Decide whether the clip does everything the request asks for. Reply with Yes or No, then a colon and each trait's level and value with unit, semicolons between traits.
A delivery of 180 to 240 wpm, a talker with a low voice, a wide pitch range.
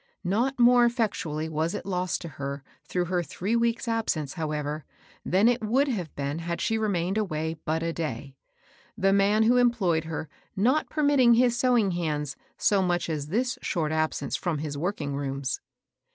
No: average, 190 wpm; medium, 180 Hz; wide, 6.5 semitones